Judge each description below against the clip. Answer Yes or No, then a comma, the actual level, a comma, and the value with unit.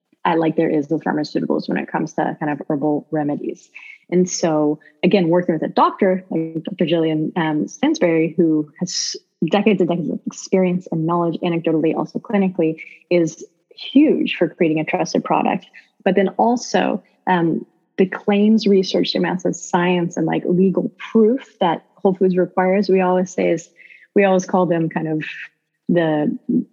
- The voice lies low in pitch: No, medium, 180 Hz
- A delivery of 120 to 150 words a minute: No, average, 165 wpm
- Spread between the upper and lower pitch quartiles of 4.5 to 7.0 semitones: No, average, 3.4 semitones